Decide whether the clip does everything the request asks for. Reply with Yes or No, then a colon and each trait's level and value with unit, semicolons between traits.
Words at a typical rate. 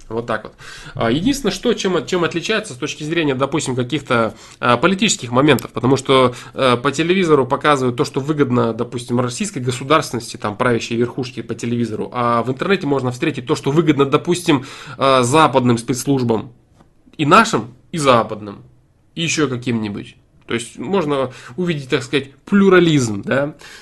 Yes: average, 145 wpm